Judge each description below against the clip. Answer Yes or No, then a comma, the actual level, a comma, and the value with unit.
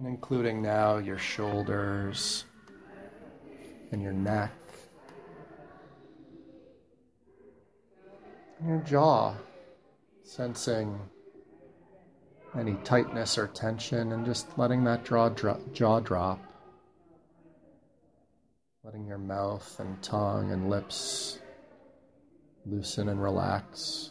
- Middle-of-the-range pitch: No, low, 105 Hz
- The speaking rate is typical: No, slow, 80 wpm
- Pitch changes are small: No, average, 3.0 semitones